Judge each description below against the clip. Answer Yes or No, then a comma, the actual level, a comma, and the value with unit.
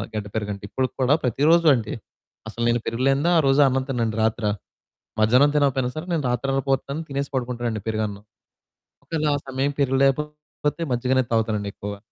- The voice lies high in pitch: No, low, 130 Hz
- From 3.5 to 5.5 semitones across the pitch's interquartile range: Yes, average, 3.8 semitones